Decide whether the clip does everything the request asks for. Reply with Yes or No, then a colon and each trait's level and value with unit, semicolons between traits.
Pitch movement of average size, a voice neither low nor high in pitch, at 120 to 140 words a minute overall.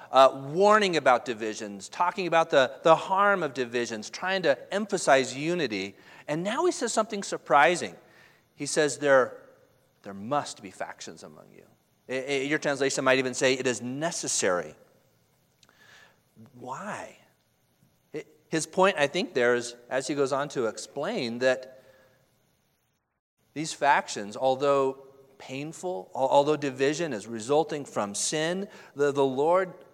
Yes: average, 4.7 semitones; medium, 145 Hz; slow, 135 wpm